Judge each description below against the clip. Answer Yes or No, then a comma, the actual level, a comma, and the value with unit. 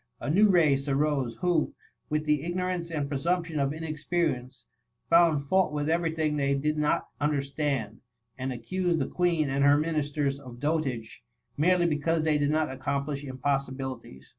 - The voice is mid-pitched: Yes, medium, 150 Hz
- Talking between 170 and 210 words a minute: No, average, 160 wpm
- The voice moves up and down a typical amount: Yes, average, 3.0 semitones